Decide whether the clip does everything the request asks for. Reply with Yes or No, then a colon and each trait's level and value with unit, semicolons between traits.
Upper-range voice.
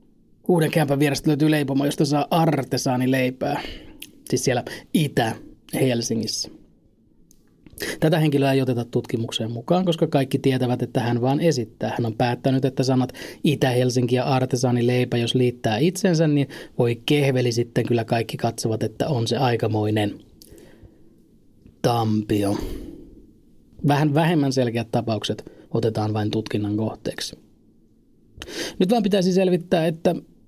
No: low, 130 Hz